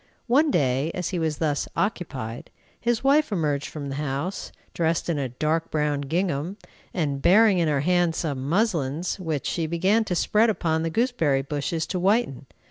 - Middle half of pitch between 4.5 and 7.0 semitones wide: Yes, average, 4.9 semitones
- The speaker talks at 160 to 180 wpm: Yes, average, 175 wpm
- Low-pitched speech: No, medium, 165 Hz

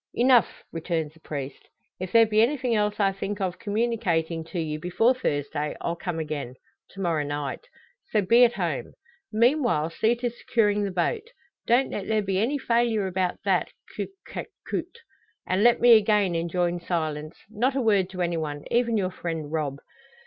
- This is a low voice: No, high, 195 Hz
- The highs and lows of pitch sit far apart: Yes, wide, 5.9 semitones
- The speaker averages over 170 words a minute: Yes, average, 180 wpm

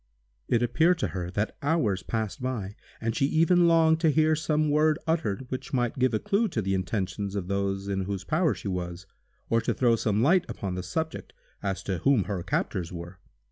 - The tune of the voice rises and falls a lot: Yes, wide, 8.1 semitones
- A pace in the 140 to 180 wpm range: No, fast, 205 wpm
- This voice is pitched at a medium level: No, low, 115 Hz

